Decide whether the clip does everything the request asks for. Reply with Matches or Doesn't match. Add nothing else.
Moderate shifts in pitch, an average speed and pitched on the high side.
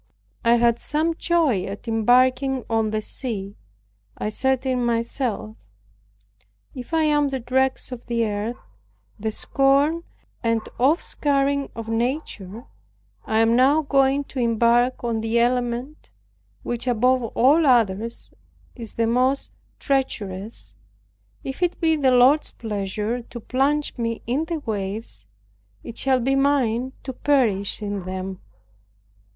Doesn't match